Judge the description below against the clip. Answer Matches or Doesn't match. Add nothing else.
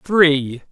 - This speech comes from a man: Matches